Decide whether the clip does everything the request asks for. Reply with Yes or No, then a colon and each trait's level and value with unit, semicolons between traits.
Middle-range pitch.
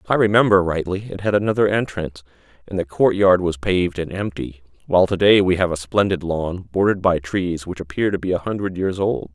No: very low, 90 Hz